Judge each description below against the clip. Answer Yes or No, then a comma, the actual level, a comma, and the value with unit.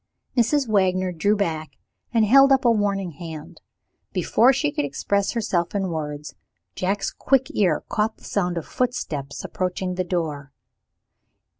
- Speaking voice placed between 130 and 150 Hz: No, medium, 185 Hz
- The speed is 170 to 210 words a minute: No, average, 145 wpm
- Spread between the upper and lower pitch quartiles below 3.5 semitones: No, average, 5.1 semitones